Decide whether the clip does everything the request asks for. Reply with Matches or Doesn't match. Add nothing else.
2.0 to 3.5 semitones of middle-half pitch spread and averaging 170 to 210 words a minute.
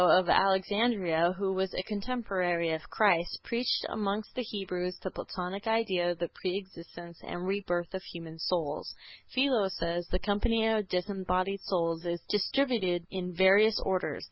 Doesn't match